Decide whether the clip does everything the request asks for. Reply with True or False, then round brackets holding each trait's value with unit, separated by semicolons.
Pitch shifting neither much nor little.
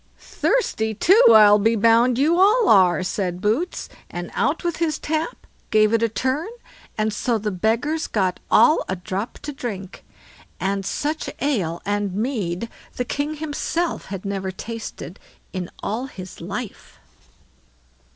False (6.9 semitones)